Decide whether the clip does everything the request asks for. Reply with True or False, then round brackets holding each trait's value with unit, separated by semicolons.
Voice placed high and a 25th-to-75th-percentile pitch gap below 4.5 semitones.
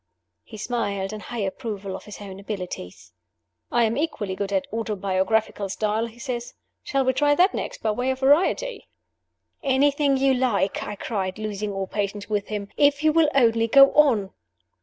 False (220 Hz; 4.9 semitones)